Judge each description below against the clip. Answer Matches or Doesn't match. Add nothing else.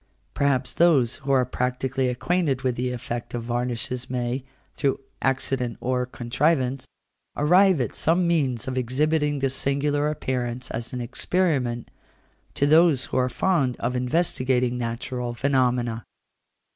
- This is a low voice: Matches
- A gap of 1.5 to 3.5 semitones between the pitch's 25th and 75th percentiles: Matches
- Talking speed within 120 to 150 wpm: Matches